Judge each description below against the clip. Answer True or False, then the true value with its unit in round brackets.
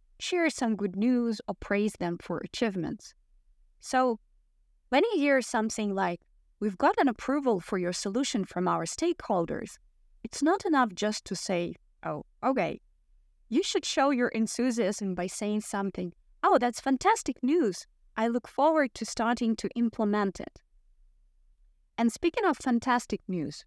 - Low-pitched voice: False (230 Hz)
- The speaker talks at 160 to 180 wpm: False (145 wpm)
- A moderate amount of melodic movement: True (5.0 semitones)